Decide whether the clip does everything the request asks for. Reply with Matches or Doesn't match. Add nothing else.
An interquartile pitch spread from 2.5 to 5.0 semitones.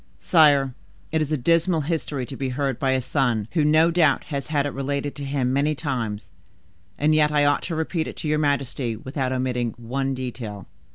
Matches